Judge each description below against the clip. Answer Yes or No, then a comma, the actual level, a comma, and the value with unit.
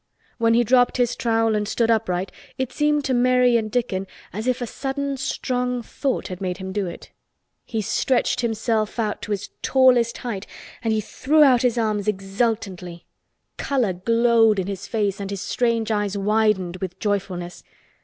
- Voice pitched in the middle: No, high, 225 Hz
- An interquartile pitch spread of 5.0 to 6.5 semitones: No, average, 3.7 semitones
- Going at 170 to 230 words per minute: Yes, average, 175 wpm